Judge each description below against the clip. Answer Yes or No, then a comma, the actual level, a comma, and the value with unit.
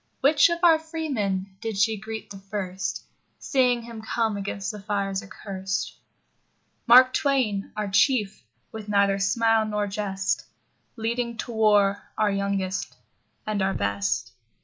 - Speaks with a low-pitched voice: No, high, 210 Hz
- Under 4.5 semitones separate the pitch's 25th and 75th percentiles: Yes, average, 2.9 semitones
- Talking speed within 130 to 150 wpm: Yes, slow, 135 wpm